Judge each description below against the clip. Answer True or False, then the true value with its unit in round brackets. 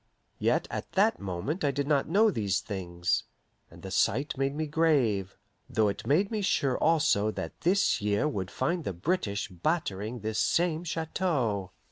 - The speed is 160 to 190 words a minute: True (165 wpm)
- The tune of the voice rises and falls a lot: True (8.3 semitones)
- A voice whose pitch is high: False (135 Hz)